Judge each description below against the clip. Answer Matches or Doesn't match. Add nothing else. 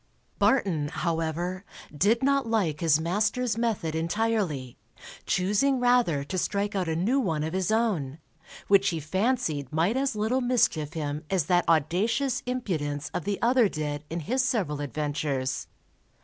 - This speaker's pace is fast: Doesn't match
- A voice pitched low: Doesn't match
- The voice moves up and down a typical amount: Doesn't match